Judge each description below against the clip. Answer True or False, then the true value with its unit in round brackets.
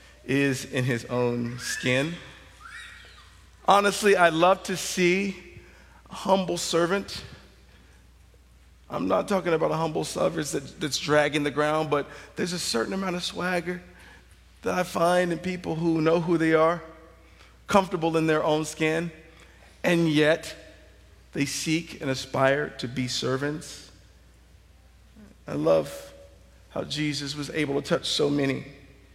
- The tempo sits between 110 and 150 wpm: True (135 wpm)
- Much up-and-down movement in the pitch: True (6.4 semitones)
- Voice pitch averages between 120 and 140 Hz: False (150 Hz)